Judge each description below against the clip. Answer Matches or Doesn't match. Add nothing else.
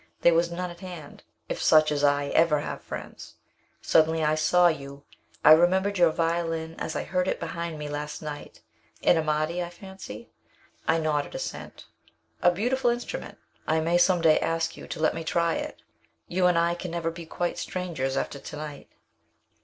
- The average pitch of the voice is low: Doesn't match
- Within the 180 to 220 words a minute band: Matches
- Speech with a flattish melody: Matches